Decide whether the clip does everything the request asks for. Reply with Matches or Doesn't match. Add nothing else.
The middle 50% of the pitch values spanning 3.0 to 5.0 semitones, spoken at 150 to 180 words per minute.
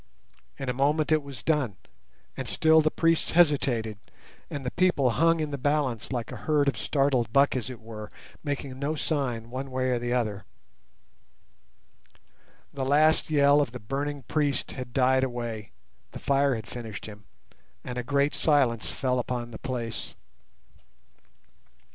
Matches